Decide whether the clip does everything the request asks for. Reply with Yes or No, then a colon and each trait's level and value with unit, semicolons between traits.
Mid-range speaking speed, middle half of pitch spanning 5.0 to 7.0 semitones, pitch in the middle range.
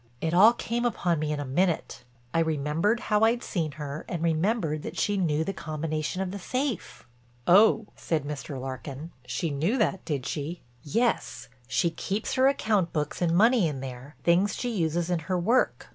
Yes: average, 180 wpm; wide, 5.6 semitones; medium, 170 Hz